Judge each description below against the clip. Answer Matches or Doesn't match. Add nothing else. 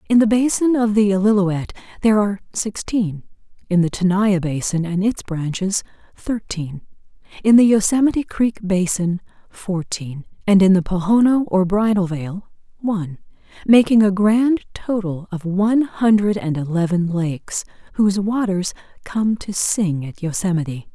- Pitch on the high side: Matches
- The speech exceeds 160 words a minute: Doesn't match